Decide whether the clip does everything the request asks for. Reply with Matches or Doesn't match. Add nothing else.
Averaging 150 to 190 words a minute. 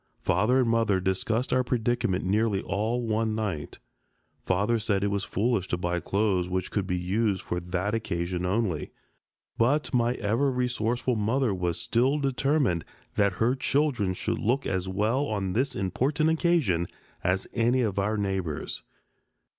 Matches